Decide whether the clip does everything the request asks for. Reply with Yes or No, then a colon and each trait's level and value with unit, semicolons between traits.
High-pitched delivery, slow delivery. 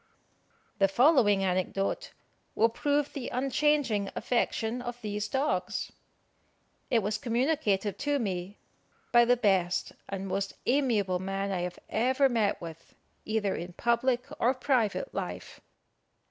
Yes: high, 220 Hz; slow, 125 wpm